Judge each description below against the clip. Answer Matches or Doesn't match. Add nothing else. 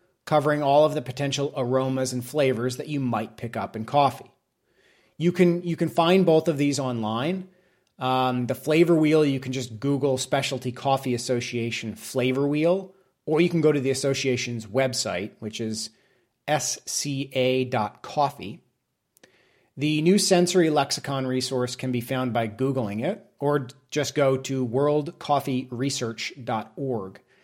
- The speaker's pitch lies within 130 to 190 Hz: Matches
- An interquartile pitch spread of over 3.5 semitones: Doesn't match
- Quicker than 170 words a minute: Doesn't match